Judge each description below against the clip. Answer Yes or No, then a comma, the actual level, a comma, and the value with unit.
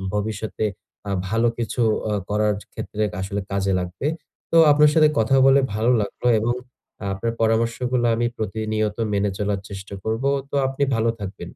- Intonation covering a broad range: No, average, 2.7 semitones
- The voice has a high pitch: No, low, 110 Hz